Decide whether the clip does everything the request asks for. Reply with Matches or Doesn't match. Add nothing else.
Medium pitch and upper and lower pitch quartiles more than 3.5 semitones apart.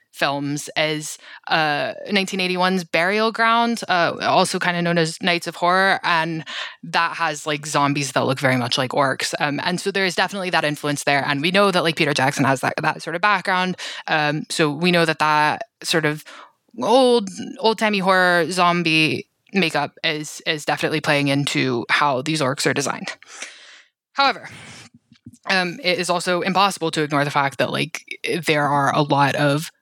Matches